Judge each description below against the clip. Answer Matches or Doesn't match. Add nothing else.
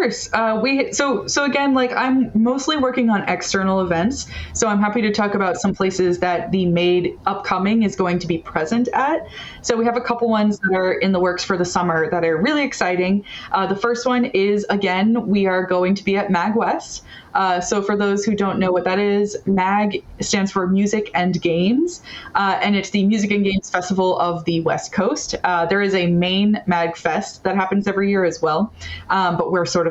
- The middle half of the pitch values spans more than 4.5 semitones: Doesn't match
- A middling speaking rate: Doesn't match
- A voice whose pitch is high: Matches